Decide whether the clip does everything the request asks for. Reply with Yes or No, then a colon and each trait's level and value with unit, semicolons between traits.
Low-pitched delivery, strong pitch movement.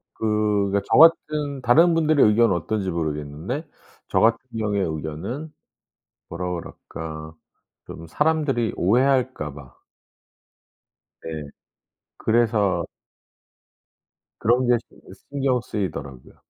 Yes: low, 105 Hz; wide, 7.9 semitones